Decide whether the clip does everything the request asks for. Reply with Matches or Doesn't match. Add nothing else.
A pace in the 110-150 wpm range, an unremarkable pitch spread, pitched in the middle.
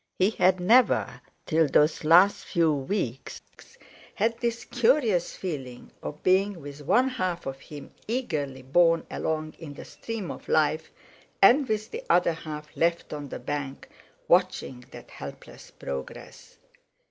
Doesn't match